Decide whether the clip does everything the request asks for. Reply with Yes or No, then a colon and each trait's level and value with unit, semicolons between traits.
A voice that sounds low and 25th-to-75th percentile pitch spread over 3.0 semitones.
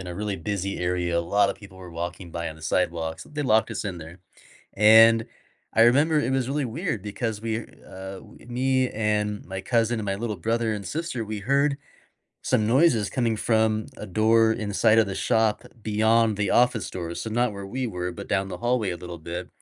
Yes: low, 105 Hz; average, 3.5 semitones